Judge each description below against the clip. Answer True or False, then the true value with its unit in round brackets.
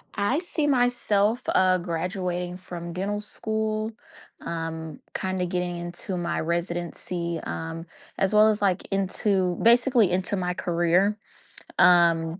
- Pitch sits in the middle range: True (180 Hz)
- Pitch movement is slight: False (3.2 semitones)